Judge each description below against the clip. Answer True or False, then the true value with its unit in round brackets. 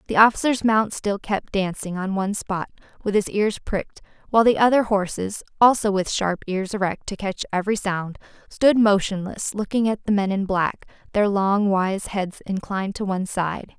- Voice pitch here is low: False (200 Hz)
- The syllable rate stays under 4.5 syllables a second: False (5.0 syllables/s)